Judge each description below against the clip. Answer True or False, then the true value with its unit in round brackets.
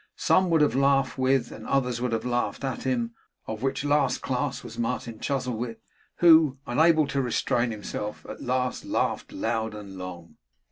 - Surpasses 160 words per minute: True (170 wpm)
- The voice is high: False (125 Hz)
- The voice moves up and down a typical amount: True (3.2 semitones)